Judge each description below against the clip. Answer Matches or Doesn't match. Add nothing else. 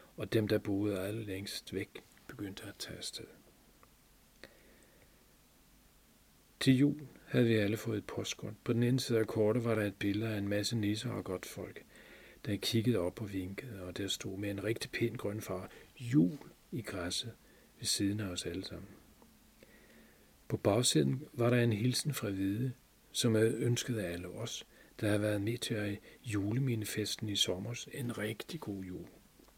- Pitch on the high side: Doesn't match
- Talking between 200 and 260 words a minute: Doesn't match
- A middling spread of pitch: Matches